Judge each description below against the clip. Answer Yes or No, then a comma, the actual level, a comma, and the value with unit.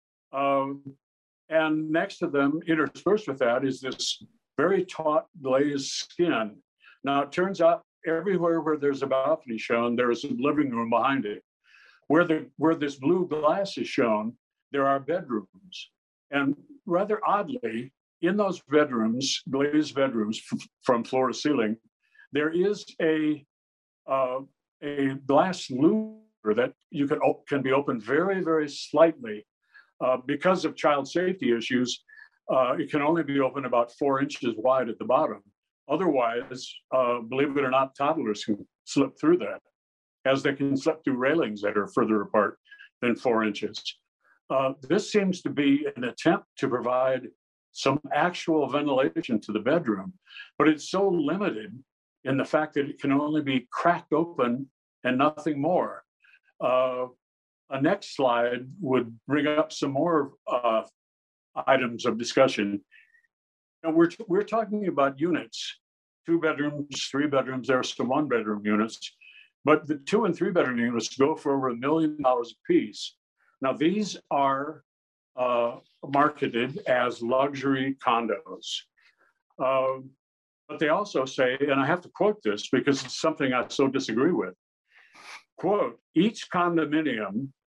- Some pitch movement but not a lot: Yes, average, 4.0 semitones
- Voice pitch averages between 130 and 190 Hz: Yes, medium, 140 Hz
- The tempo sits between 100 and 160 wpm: Yes, average, 150 wpm